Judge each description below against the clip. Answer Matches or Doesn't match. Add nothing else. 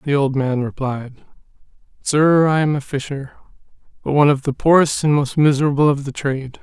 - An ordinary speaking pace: Matches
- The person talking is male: Matches